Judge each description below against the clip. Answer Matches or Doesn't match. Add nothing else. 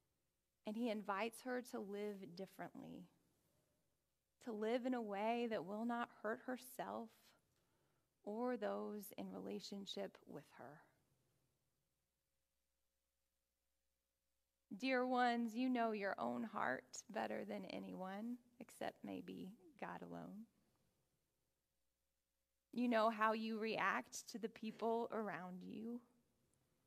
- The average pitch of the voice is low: Doesn't match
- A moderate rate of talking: Doesn't match